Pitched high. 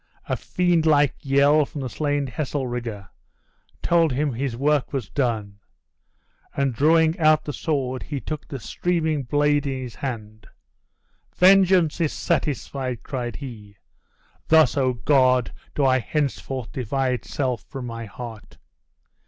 No: low, 135 Hz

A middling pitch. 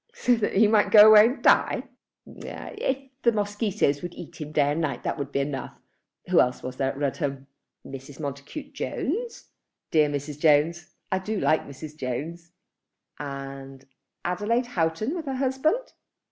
Yes: medium, 165 Hz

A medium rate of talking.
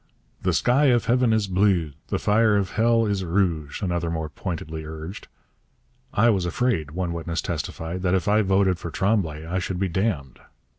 Yes: average, 180 wpm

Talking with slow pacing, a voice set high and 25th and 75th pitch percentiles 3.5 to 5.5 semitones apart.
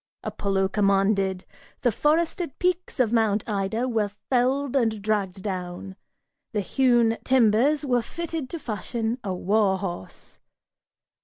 Yes: slow, 125 wpm; high, 220 Hz; average, 4.6 semitones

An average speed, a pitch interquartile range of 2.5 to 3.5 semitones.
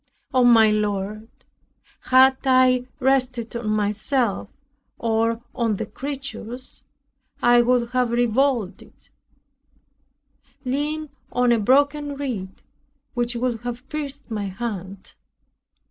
No: slow, 100 wpm; average, 3.1 semitones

